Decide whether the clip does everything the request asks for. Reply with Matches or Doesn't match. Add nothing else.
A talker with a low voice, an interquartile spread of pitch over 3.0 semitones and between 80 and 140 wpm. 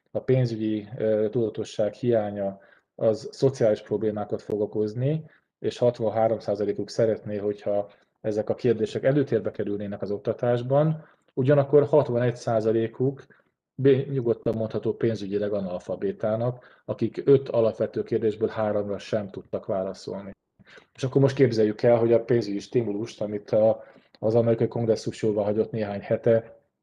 Doesn't match